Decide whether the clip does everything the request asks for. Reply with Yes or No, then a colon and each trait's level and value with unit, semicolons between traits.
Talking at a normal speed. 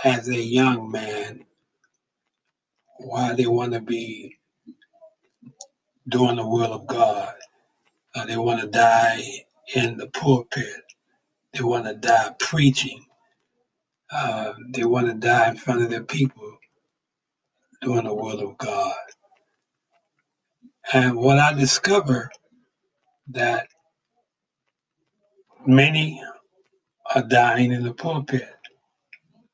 No: slow, 110 wpm